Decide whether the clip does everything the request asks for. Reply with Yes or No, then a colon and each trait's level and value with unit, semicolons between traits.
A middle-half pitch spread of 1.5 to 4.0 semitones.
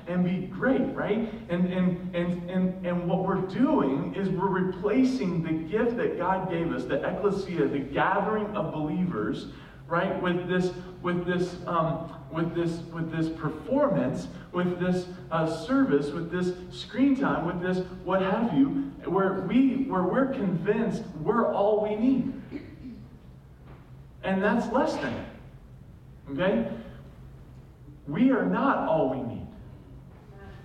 Yes: average, 3.3 semitones